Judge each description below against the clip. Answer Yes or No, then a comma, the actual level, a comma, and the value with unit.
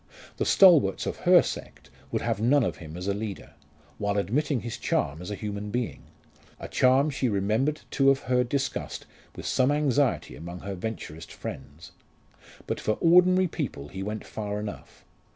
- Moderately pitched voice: No, low, 110 Hz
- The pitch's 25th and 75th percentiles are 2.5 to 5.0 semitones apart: No, wide, 5.6 semitones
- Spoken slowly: No, average, 170 wpm